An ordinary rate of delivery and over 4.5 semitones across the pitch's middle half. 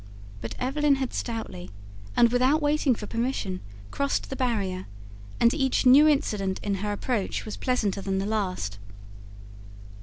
Yes: average, 145 wpm; average, 5.3 semitones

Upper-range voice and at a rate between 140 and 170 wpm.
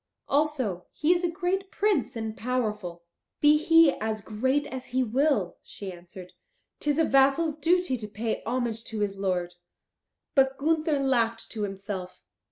Yes: very high, 255 Hz; average, 160 wpm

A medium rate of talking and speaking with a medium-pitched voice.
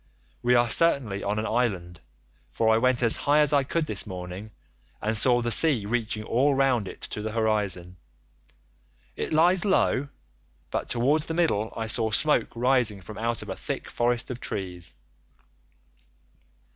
No: average, 165 wpm; low, 115 Hz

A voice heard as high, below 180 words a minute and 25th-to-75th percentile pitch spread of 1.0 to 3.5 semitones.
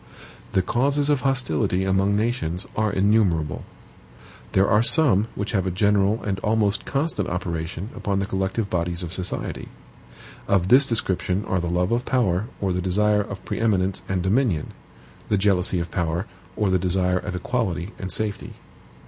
No: very low, 95 Hz; average, 165 wpm; average, 3.1 semitones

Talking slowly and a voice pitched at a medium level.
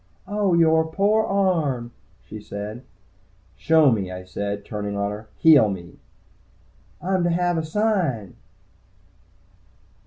Yes: slow, 120 wpm; medium, 150 Hz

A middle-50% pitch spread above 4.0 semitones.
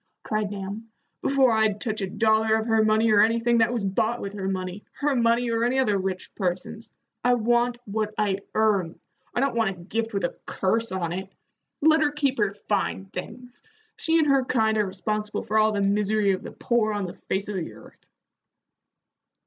No: average, 3.0 semitones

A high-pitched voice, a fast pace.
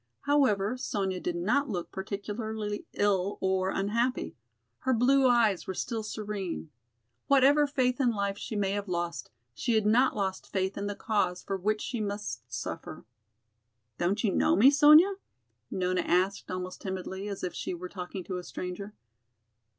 No: high, 205 Hz; average, 160 wpm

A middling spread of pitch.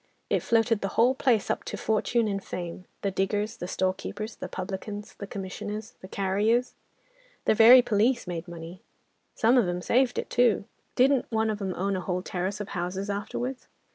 Yes: average, 3.4 semitones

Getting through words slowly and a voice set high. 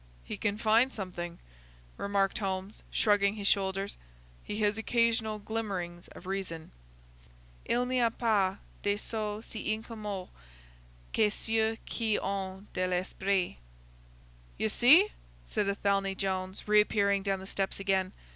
Yes: slow, 130 wpm; high, 200 Hz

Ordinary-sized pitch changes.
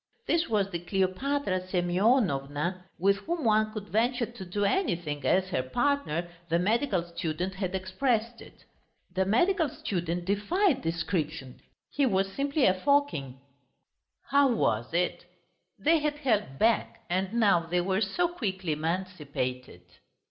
No: wide, 5.8 semitones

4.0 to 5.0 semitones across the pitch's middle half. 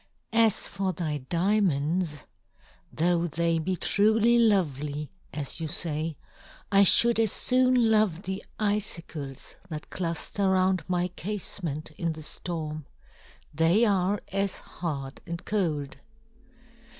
Yes: average, 4.6 semitones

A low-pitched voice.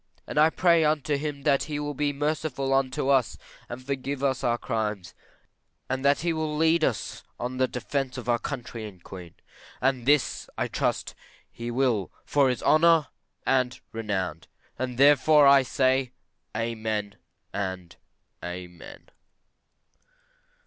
Yes: low, 130 Hz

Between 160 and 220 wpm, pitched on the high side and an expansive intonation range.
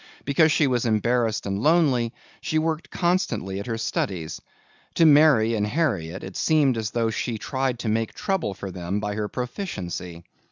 No: average, 170 wpm; low, 115 Hz; wide, 6.5 semitones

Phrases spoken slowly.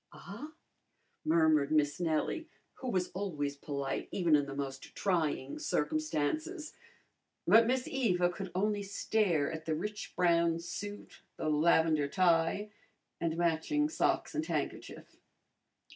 Yes: slow, 125 wpm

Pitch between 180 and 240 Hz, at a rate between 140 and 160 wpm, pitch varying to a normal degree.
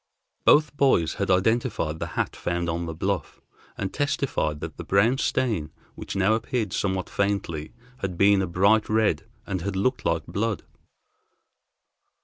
No: low, 100 Hz; average, 150 wpm; average, 4.4 semitones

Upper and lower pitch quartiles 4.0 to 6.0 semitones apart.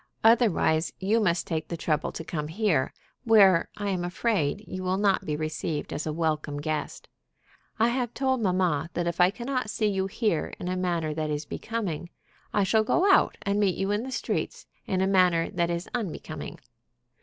Yes: average, 4.8 semitones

